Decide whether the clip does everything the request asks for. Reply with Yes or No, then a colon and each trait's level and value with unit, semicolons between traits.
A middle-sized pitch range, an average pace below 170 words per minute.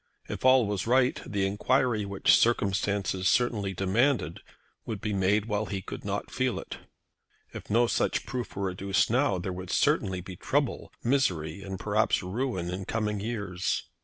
Yes: average, 3.8 semitones; average, 160 wpm